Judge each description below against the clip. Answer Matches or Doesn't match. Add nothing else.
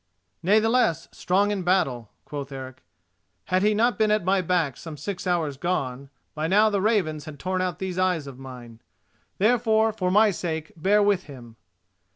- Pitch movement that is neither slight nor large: Doesn't match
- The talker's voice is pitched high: Doesn't match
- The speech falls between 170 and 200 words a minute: Matches